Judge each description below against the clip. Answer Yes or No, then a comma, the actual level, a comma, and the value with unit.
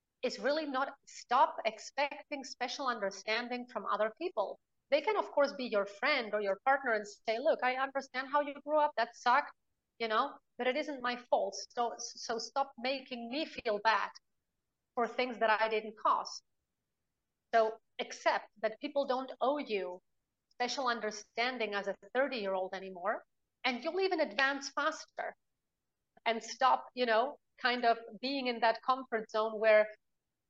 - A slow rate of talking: No, average, 160 wpm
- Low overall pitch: No, high, 245 Hz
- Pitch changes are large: No, average, 3.9 semitones